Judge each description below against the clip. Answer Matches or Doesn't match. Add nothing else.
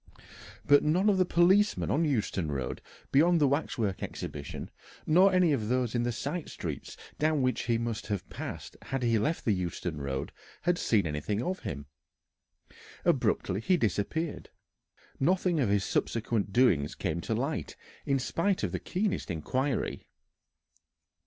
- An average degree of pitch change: Doesn't match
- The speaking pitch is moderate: Doesn't match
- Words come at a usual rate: Matches